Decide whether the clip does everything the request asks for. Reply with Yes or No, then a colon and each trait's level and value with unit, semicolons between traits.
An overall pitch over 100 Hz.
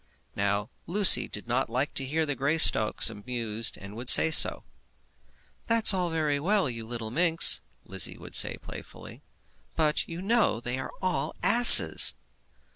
Yes: medium, 140 Hz